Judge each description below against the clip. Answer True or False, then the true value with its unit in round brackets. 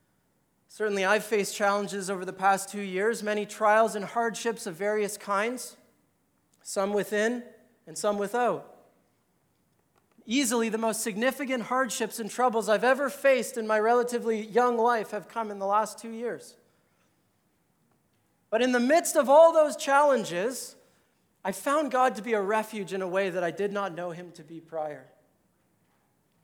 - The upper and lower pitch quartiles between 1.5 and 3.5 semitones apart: True (3.2 semitones)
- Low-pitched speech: False (220 Hz)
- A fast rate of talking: False (160 wpm)